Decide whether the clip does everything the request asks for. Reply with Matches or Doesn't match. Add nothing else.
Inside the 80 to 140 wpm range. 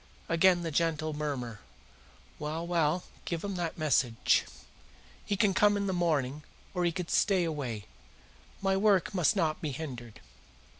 Doesn't match